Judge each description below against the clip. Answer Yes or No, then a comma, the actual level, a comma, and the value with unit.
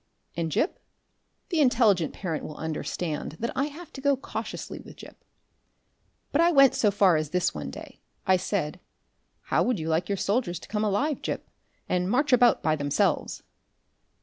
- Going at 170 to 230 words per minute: Yes, average, 175 wpm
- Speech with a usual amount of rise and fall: No, wide, 7.9 semitones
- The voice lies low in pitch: No, high, 200 Hz